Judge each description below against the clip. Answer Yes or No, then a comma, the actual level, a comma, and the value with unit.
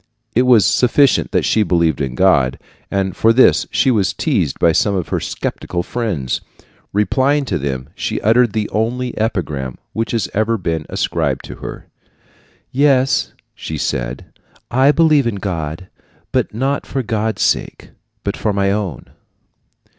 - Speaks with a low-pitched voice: Yes, low, 105 Hz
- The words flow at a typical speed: Yes, average, 150 wpm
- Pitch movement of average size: No, wide, 6.7 semitones